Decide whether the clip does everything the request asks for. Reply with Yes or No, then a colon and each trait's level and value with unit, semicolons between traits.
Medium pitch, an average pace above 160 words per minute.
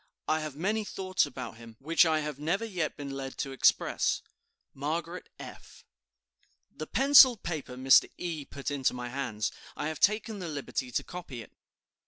Yes: medium, 150 Hz; average, 170 wpm